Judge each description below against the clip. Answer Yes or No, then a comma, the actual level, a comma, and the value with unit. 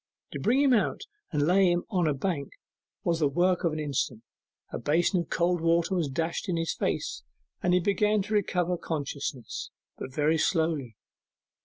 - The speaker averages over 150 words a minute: Yes, average, 180 wpm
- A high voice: No, medium, 170 Hz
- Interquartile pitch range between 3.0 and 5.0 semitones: Yes, average, 3.3 semitones